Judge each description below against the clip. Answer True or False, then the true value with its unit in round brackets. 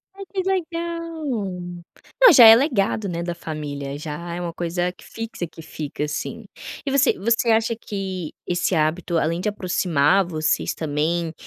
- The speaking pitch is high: False (180 Hz)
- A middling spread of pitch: False (6.1 semitones)